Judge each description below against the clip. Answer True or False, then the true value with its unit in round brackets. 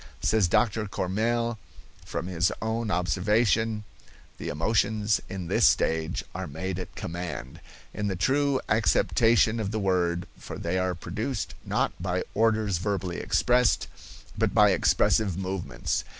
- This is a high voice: False (100 Hz)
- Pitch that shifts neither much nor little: True (3.6 semitones)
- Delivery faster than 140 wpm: False (135 wpm)